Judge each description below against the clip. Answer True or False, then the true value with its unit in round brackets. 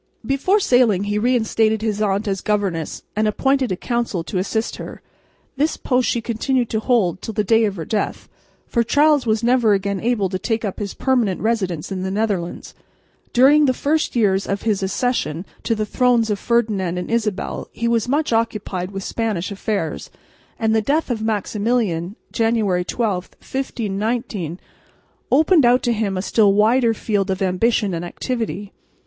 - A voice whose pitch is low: False (220 Hz)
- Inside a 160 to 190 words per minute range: True (170 wpm)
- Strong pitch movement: False (3.5 semitones)